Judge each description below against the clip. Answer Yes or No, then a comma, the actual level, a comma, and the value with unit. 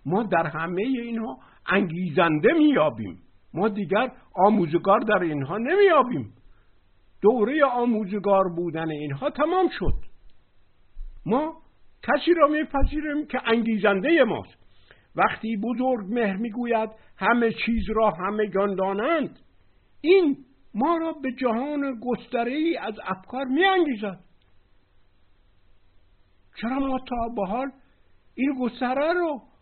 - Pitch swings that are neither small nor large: No, wide, 8.0 semitones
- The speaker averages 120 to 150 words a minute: No, slow, 105 wpm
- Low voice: No, high, 220 Hz